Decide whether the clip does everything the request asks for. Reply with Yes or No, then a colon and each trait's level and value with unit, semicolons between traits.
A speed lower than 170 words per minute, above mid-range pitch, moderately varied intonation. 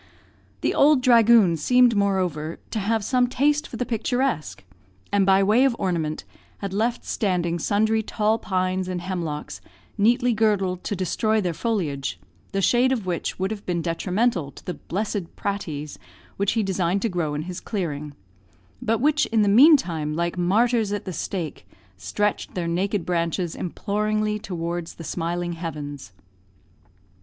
Yes: average, 155 wpm; high, 195 Hz; average, 4.4 semitones